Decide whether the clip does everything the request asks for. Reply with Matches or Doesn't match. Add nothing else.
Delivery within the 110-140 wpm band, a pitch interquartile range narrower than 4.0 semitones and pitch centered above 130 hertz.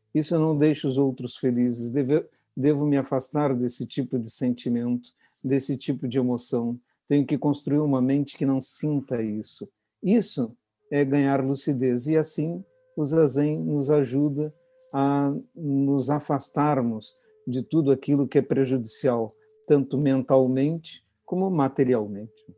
Matches